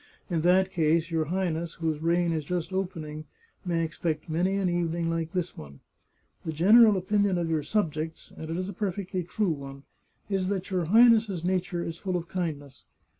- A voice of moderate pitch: Yes, medium, 175 Hz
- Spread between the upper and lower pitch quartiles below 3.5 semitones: Yes, average, 2.8 semitones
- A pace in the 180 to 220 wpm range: Yes, average, 185 wpm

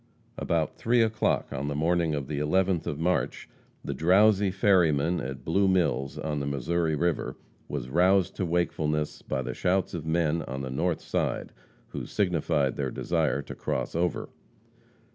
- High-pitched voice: No, very low, 80 Hz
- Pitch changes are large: No, average, 3.9 semitones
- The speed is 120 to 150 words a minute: No, average, 160 wpm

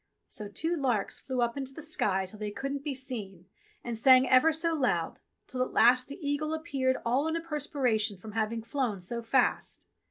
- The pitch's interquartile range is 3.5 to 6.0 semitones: Yes, average, 4.5 semitones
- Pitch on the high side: Yes, very high, 255 Hz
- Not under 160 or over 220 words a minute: Yes, average, 195 wpm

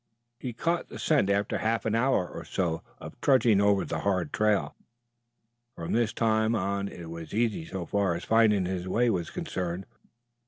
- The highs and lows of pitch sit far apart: No, average, 3.6 semitones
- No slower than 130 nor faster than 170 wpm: No, average, 180 wpm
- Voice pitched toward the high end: No, low, 100 Hz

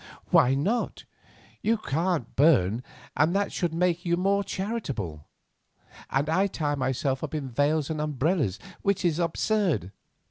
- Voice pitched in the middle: Yes, medium, 155 Hz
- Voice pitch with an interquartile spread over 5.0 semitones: Yes, wide, 5.4 semitones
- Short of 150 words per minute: Yes, average, 140 wpm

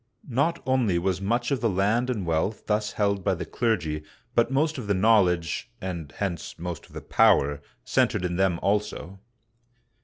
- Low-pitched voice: Yes, low, 100 Hz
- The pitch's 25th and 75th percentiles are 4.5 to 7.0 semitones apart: Yes, average, 4.8 semitones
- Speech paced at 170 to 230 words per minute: Yes, average, 185 wpm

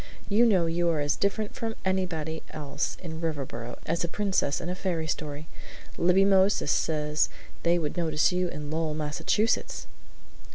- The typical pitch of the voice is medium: Yes, medium, 165 Hz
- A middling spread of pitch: Yes, average, 3.7 semitones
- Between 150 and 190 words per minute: Yes, average, 160 wpm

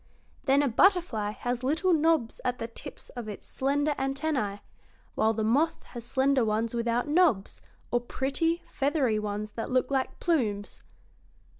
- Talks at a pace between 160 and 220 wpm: No, average, 150 wpm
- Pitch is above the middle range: Yes, very high, 255 Hz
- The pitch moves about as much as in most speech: Yes, average, 4.6 semitones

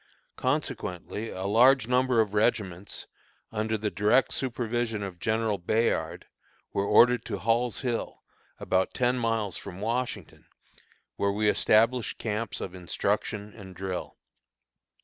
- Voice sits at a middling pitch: No, low, 110 Hz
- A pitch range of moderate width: Yes, average, 3.1 semitones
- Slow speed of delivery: Yes, slow, 125 wpm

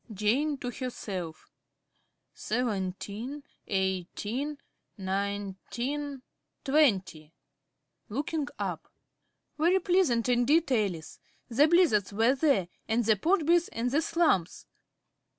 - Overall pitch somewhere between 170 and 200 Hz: No, high, 240 Hz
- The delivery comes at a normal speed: No, slow, 90 wpm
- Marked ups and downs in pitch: Yes, wide, 6.7 semitones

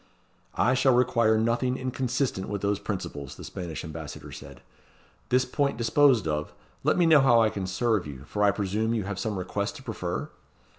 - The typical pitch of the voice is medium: No, low, 110 Hz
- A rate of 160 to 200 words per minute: Yes, average, 185 wpm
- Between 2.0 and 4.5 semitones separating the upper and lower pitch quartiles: No, average, 5.0 semitones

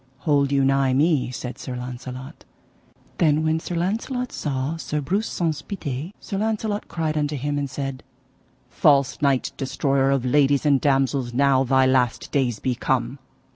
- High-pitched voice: No, medium, 140 Hz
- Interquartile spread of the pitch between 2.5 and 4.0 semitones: Yes, average, 2.9 semitones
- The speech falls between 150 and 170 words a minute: Yes, average, 160 wpm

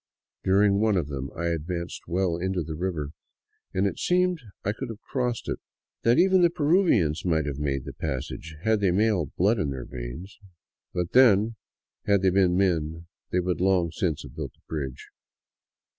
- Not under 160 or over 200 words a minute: Yes, average, 180 wpm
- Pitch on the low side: Yes, very low, 90 Hz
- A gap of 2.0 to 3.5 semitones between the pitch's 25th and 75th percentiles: No, average, 5.0 semitones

